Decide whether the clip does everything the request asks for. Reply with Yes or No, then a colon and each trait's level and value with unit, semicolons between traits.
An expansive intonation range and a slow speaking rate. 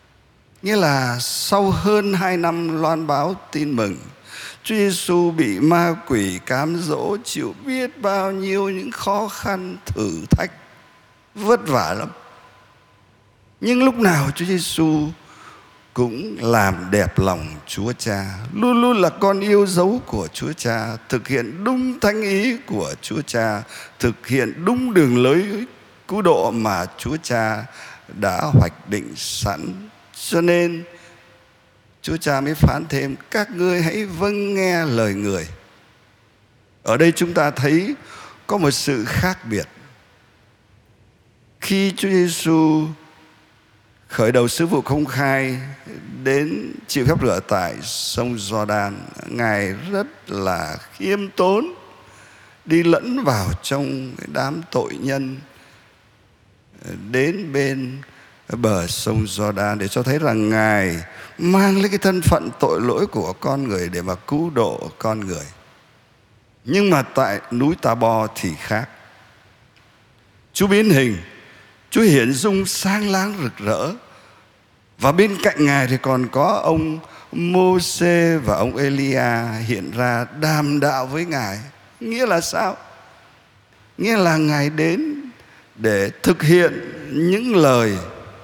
Yes: wide, 8.4 semitones; slow, 135 wpm